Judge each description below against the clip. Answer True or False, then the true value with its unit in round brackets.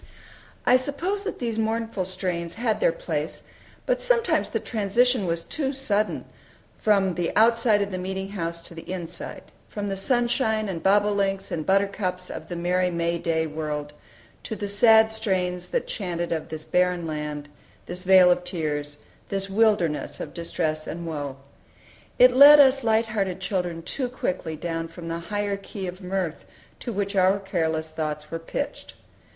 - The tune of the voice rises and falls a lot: False (4.6 semitones)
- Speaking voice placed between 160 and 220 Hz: True (190 Hz)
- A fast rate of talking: False (165 wpm)